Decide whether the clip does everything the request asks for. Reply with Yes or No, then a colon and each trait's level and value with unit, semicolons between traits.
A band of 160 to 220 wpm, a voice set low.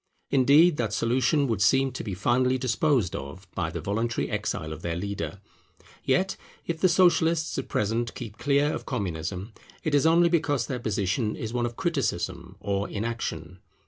Yes: average, 170 wpm; low, 120 Hz